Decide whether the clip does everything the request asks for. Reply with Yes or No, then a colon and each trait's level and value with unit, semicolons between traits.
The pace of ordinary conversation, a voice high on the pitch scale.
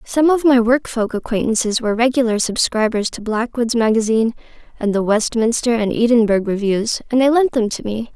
Yes: average, 175 wpm; high, 230 Hz